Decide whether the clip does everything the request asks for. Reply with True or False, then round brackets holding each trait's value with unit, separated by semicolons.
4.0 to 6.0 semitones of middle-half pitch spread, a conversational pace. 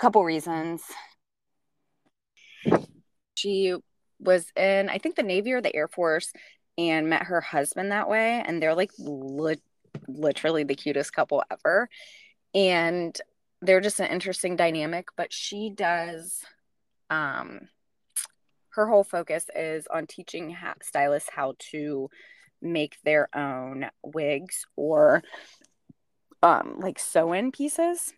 False (4.3 semitones; 120 wpm)